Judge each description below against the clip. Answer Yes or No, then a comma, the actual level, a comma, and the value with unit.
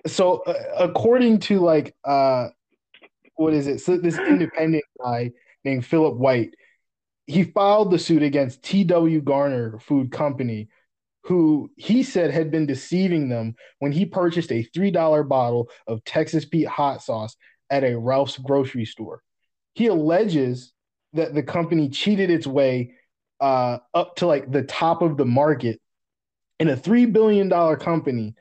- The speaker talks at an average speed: Yes, average, 145 wpm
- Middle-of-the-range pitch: Yes, medium, 150 Hz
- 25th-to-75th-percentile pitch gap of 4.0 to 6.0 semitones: Yes, average, 4.8 semitones